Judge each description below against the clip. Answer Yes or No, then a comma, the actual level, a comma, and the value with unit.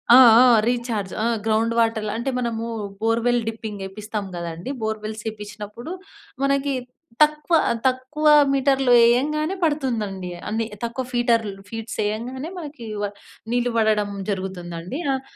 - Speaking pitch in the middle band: No, high, 230 Hz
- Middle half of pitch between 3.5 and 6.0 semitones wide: Yes, average, 3.8 semitones